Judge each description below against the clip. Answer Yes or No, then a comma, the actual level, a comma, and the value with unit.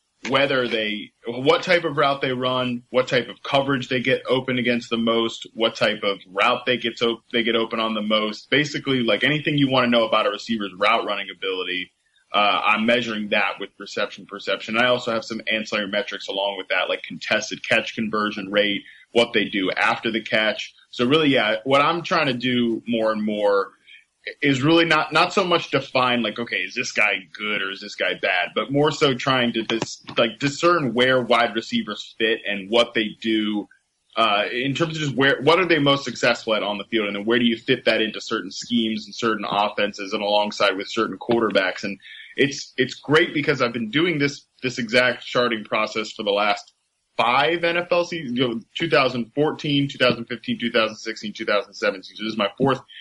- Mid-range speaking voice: No, low, 120 Hz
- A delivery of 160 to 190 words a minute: No, fast, 205 wpm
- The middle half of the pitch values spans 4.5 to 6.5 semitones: No, average, 3.8 semitones